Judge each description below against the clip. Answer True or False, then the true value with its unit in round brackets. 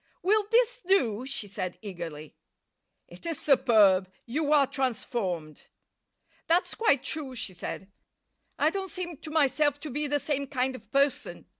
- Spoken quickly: False (150 wpm)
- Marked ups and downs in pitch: True (6.5 semitones)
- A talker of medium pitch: False (275 Hz)